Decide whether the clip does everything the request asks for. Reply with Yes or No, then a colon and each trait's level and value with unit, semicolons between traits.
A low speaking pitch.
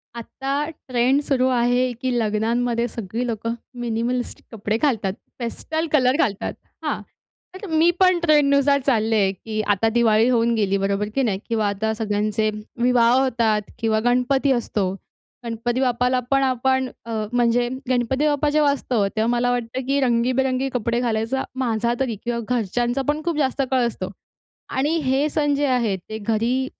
No: high, 245 Hz